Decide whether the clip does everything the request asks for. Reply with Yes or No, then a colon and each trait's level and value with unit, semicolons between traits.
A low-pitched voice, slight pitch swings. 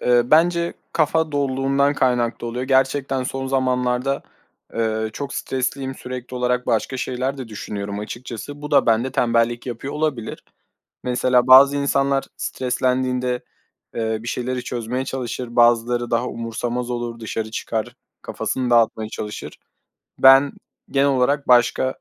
Yes: low, 125 Hz; narrow, 2.2 semitones